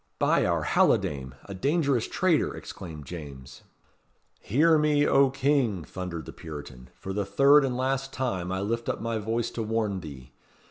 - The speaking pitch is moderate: No, low, 110 Hz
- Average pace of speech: Yes, average, 165 wpm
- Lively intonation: Yes, wide, 7.8 semitones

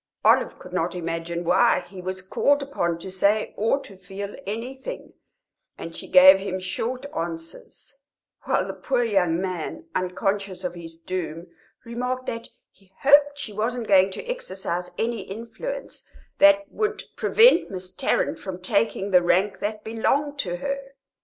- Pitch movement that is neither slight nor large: No, wide, 5.8 semitones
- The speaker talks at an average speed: Yes, average, 155 wpm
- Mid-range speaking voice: No, high, 200 Hz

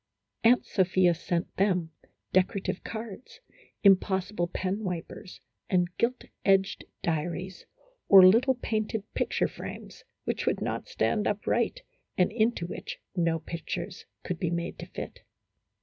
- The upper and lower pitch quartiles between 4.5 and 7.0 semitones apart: No, average, 3.5 semitones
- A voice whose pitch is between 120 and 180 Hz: No, high, 190 Hz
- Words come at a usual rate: No, slow, 120 wpm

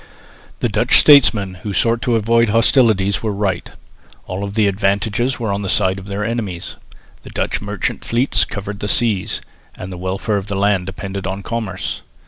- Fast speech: No, average, 175 wpm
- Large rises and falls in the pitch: No, average, 2.9 semitones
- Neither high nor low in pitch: No, low, 100 Hz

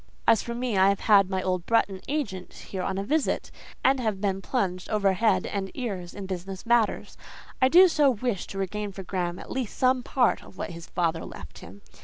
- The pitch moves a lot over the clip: No, average, 4.3 semitones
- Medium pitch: No, high, 200 Hz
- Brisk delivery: Yes, fast, 210 wpm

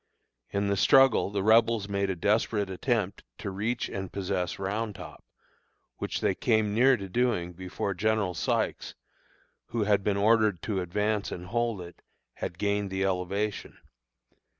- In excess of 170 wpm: No, average, 150 wpm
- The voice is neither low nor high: No, low, 100 Hz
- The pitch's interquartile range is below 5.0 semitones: Yes, narrow, 2.4 semitones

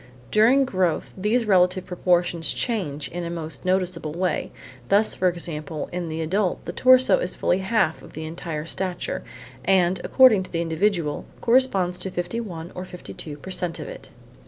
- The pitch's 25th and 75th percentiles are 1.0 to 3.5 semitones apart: Yes, average, 2.8 semitones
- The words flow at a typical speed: Yes, average, 165 wpm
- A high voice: No, medium, 180 Hz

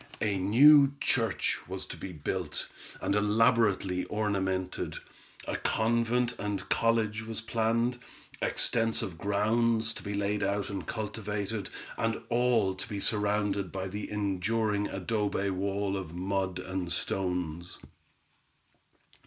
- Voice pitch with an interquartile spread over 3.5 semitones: No, average, 2.9 semitones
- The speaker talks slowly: Yes, slow, 120 wpm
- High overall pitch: No, low, 105 Hz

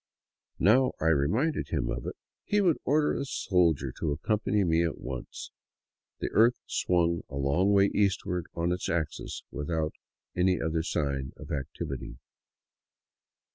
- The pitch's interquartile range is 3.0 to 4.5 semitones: No, average, 5.3 semitones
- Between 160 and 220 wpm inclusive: No, average, 140 wpm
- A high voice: No, very low, 85 Hz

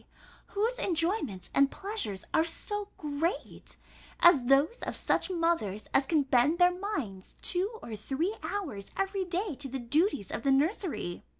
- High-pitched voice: Yes, very high, 325 Hz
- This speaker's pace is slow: No, average, 155 wpm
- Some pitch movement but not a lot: No, wide, 6.2 semitones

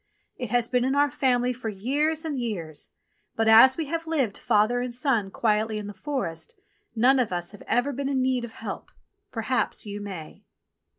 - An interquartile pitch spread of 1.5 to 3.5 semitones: No, average, 4.2 semitones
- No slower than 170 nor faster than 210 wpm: Yes, average, 195 wpm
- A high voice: Yes, high, 245 Hz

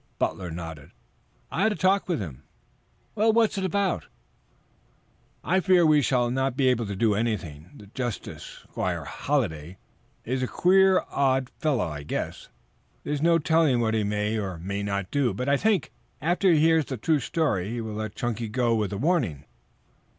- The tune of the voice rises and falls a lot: Yes, wide, 8.1 semitones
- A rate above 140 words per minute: Yes, average, 180 wpm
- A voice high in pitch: No, low, 125 Hz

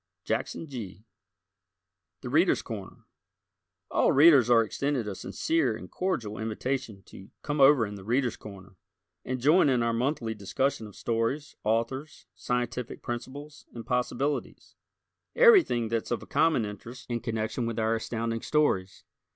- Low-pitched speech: Yes, low, 120 Hz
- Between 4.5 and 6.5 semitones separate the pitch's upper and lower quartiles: No, average, 3.9 semitones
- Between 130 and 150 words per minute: Yes, average, 140 wpm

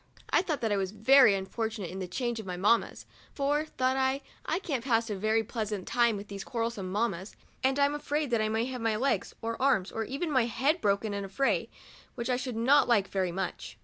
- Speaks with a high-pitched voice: Yes, high, 230 Hz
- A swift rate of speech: Yes, fast, 235 wpm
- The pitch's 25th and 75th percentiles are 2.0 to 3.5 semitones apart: No, average, 4.6 semitones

